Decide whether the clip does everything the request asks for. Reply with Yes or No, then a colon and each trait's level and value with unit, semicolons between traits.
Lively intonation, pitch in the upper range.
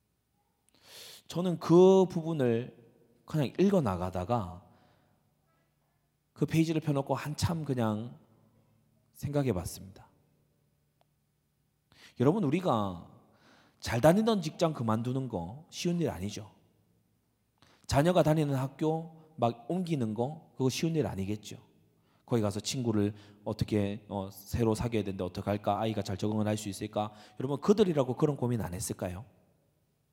No: wide, 6.1 semitones; low, 120 Hz